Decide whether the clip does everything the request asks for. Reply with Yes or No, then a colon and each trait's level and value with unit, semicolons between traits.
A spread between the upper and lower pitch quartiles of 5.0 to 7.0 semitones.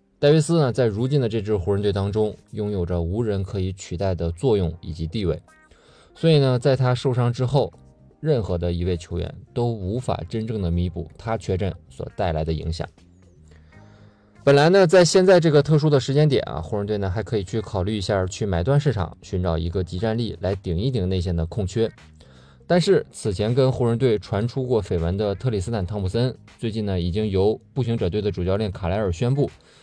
Yes: wide, 5.5 semitones